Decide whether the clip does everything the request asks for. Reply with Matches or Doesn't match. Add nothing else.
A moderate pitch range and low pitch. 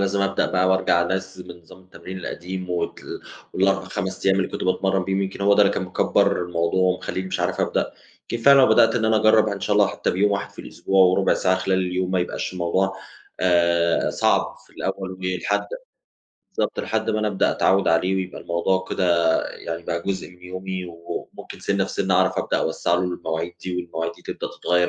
Doesn't match